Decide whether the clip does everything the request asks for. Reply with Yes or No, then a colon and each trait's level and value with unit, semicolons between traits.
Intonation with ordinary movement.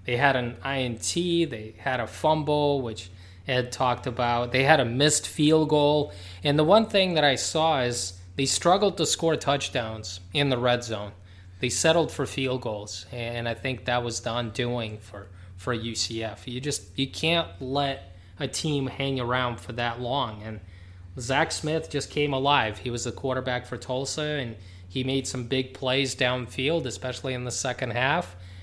Yes: average, 4.1 semitones